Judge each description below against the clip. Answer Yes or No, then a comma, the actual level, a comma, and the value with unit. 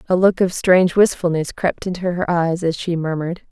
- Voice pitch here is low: No, medium, 175 Hz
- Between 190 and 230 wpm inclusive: Yes, fast, 205 wpm